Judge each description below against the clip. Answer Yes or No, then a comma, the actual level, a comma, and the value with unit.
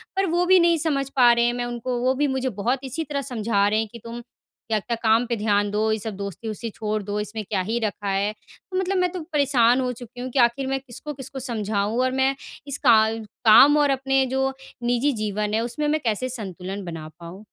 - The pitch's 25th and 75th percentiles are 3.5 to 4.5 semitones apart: Yes, average, 3.9 semitones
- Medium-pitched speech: No, high, 240 Hz